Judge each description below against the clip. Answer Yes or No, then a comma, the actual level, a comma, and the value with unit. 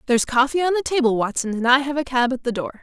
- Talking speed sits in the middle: No, fast, 300 wpm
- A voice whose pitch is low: No, very high, 260 Hz